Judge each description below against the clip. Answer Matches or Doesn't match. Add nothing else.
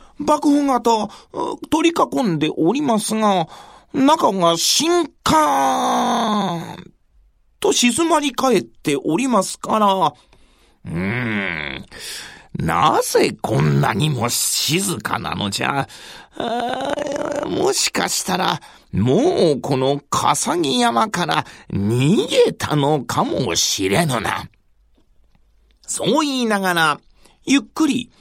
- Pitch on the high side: Matches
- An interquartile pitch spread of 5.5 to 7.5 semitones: Doesn't match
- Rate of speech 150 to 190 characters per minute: Matches